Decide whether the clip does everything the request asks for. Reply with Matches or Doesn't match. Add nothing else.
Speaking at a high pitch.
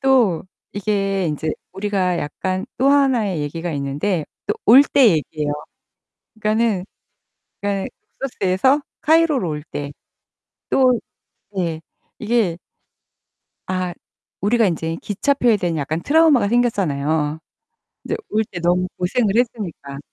Matches